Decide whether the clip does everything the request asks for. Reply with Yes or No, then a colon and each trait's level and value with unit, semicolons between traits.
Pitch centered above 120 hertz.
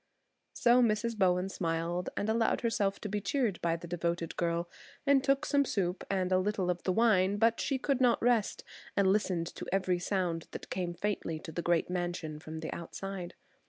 Yes: high, 190 Hz